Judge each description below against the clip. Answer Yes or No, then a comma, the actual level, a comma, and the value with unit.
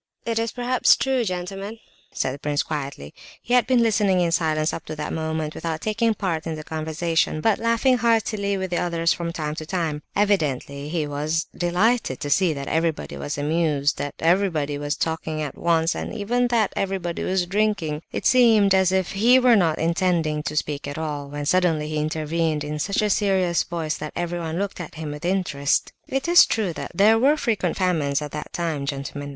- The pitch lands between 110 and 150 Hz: No, medium, 170 Hz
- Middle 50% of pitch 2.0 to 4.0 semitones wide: No, average, 4.8 semitones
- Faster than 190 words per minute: Yes, average, 200 wpm